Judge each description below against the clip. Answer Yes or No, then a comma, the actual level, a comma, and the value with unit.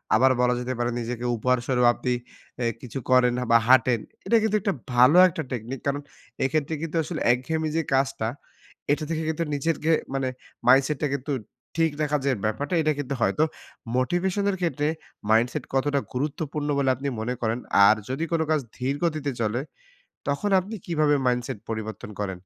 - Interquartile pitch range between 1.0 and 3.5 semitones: No, average, 4.0 semitones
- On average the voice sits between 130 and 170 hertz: Yes, low, 135 Hz